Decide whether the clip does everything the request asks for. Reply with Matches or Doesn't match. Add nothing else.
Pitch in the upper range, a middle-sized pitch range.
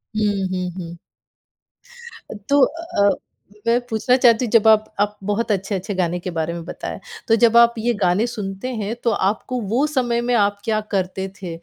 Matches